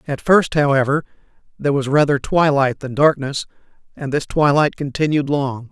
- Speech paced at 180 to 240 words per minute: No, average, 145 wpm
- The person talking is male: Yes, male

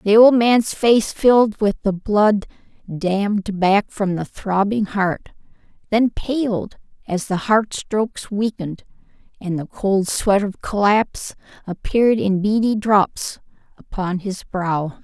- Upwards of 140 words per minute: No, slow, 135 wpm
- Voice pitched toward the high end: Yes, high, 205 Hz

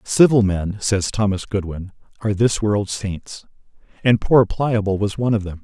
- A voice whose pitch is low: Yes, low, 105 Hz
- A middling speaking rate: Yes, average, 170 wpm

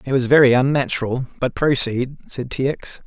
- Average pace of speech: Yes, average, 175 wpm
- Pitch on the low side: Yes, low, 130 Hz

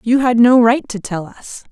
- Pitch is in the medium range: No, high, 235 Hz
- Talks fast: Yes, fast, 245 wpm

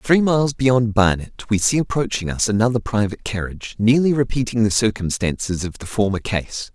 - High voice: No, low, 110 Hz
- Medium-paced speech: Yes, average, 170 wpm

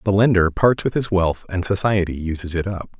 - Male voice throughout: Yes, male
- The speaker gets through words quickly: Yes, fast, 220 wpm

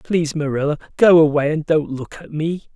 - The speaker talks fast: No, average, 195 wpm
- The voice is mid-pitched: Yes, medium, 155 Hz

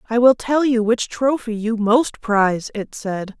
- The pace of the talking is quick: No, average, 195 wpm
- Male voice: No, female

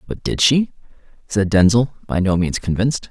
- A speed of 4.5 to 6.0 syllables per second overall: Yes, 5.2 syllables/s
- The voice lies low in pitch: Yes, low, 105 Hz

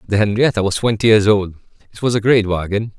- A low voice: Yes, low, 105 Hz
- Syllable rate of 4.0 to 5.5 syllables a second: No, 6.1 syllables/s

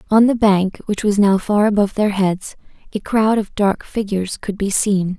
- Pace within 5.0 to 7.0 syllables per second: No, 4.8 syllables/s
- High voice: Yes, high, 205 Hz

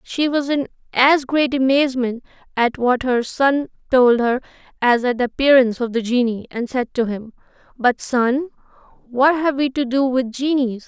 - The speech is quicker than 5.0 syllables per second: No, 4.7 syllables/s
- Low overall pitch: No, very high, 255 Hz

